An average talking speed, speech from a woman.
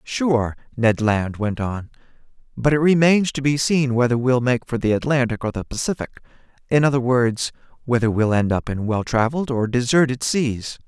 No: average, 180 wpm; male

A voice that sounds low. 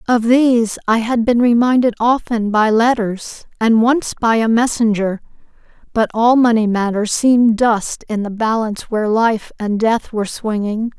No: high, 225 Hz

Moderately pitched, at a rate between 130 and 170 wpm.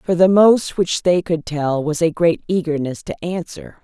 No: medium, 170 Hz; fast, 205 wpm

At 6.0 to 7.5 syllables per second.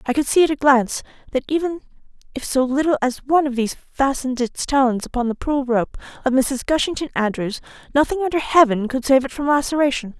Yes: 6.2 syllables/s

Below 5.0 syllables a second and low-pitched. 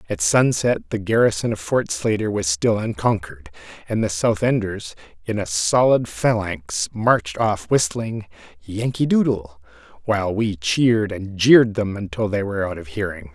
Yes: 4.8 syllables/s; low, 110 Hz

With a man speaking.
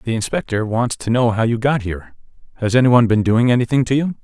Yes: male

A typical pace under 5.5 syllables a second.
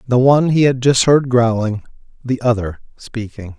Yes: 4.8 syllables/s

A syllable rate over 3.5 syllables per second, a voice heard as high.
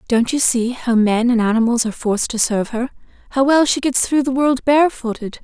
Yes: 5.8 syllables/s; high, 245 Hz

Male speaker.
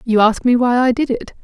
No: female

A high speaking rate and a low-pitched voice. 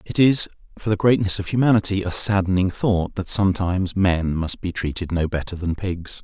No: average, 190 wpm; very low, 95 Hz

